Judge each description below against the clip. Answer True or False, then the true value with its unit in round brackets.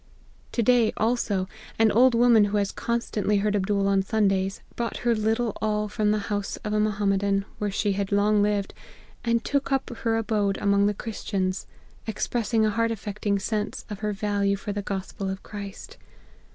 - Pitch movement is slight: True (1.9 semitones)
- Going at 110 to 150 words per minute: False (190 wpm)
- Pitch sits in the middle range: False (210 Hz)